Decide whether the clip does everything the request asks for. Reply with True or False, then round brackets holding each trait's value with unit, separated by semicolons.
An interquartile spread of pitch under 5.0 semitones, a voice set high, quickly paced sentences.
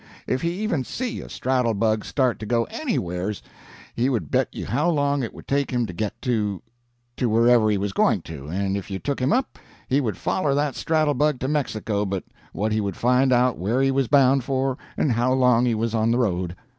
False (4.3 semitones; 120 Hz; 225 wpm)